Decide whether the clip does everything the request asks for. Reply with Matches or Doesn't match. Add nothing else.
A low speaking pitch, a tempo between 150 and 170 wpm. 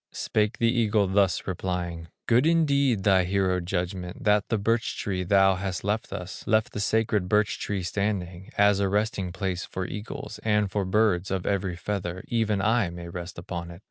Doesn't match